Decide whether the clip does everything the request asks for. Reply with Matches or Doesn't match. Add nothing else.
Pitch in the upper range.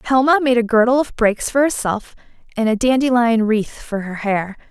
Matches